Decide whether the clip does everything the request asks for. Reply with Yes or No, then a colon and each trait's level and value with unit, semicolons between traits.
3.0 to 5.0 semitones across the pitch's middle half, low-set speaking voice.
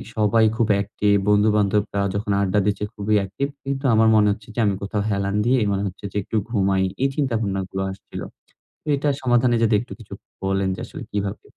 No: narrow, 2.4 semitones; low, 105 Hz